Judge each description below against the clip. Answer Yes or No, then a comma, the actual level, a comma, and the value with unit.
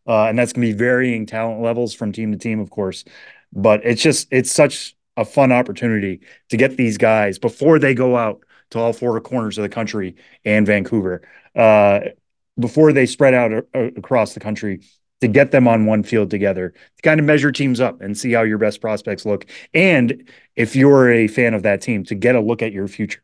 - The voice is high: No, low, 115 Hz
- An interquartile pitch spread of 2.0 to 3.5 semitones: Yes, average, 2.9 semitones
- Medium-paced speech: No, fast, 220 wpm